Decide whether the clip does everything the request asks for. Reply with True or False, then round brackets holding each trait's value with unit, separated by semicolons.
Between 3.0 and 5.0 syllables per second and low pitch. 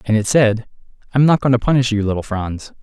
False (5.9 syllables/s; 115 Hz)